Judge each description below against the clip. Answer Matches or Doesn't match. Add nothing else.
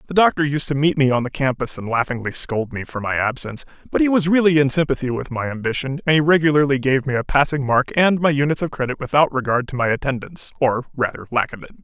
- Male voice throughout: Matches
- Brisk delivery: Matches